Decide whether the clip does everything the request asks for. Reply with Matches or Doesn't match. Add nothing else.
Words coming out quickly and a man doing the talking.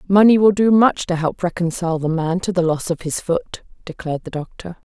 Doesn't match